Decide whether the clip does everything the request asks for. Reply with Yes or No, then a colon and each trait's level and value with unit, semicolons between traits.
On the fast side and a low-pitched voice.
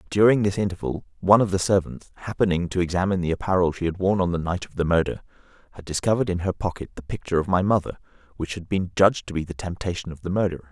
Yes: fast, 235 wpm; very low, 90 Hz